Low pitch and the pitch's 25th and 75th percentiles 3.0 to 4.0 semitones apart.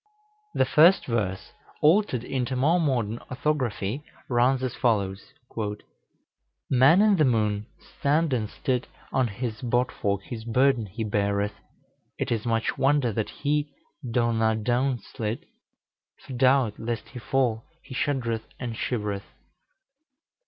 Yes: low, 120 Hz; average, 3.5 semitones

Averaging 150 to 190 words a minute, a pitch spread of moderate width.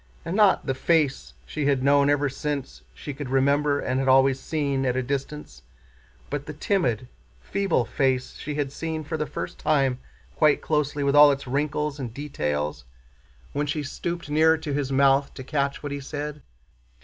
No: average, 180 wpm; narrow, 2.0 semitones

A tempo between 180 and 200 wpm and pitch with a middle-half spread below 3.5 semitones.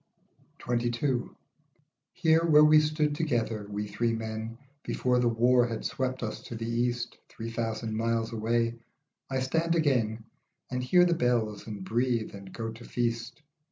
No: average, 155 wpm; narrow, 2.5 semitones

